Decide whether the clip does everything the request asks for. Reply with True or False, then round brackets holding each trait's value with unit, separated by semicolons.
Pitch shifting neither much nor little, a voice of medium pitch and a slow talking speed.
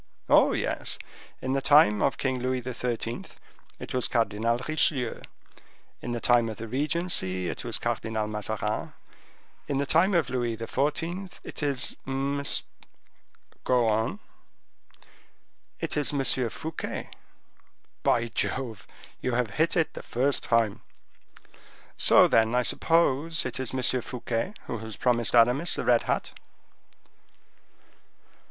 False (3.7 semitones; 125 Hz; 130 wpm)